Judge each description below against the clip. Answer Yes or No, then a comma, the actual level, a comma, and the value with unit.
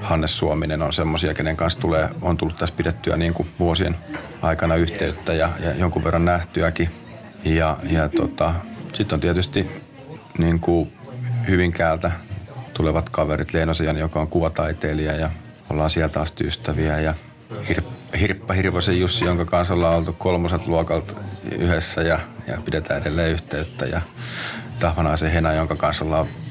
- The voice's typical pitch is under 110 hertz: Yes, very low, 85 Hz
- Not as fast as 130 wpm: No, average, 145 wpm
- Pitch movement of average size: No, narrow, 2.2 semitones